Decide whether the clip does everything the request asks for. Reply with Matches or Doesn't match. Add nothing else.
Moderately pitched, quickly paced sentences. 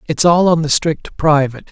Matches